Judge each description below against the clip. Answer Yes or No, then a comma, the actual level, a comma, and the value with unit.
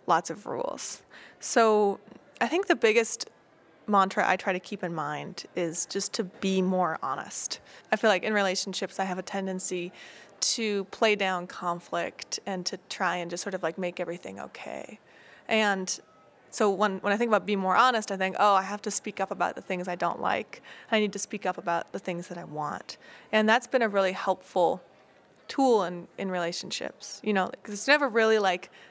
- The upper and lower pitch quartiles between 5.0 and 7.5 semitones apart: No, average, 2.7 semitones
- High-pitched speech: Yes, high, 195 Hz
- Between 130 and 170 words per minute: No, average, 200 wpm